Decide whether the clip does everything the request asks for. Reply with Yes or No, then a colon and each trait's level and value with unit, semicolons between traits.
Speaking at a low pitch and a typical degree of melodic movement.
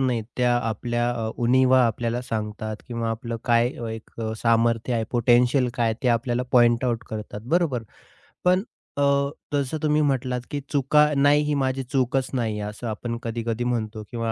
No: low, 120 Hz; narrow, 2.3 semitones